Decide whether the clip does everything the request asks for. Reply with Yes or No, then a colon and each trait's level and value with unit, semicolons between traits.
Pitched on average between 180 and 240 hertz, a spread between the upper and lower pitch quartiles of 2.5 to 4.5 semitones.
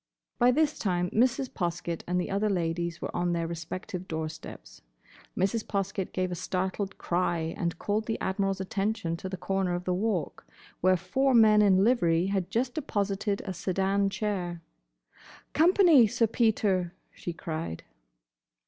Yes: high, 190 Hz; average, 3.4 semitones